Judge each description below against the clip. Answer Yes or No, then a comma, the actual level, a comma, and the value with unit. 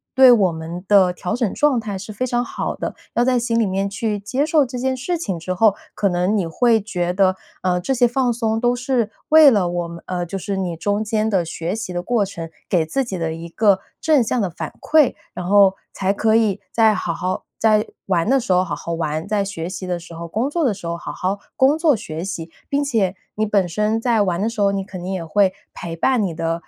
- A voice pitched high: Yes, high, 200 Hz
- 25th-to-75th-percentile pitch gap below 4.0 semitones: No, average, 4.7 semitones